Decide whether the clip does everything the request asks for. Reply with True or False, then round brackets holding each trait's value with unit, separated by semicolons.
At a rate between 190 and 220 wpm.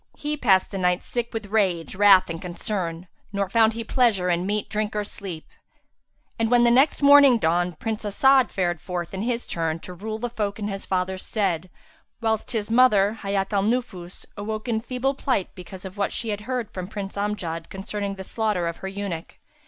True (200 wpm)